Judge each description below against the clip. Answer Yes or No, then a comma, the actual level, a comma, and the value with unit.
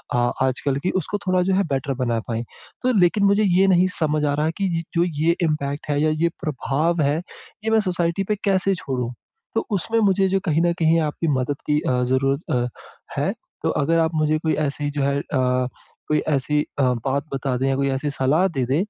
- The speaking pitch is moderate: Yes, medium, 155 Hz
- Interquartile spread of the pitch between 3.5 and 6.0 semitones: Yes, average, 4.5 semitones